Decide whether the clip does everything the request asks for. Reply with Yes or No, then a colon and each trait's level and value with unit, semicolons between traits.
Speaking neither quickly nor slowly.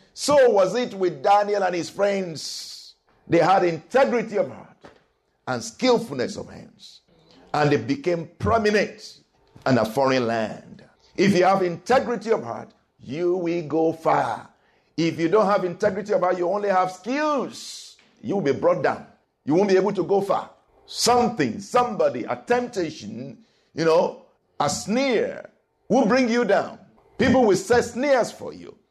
Yes: average, 160 wpm